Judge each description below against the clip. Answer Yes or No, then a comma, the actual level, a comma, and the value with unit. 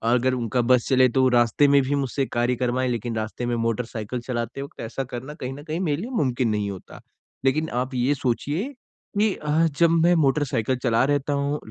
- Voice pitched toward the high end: No, low, 130 Hz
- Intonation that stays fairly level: No, average, 3.2 semitones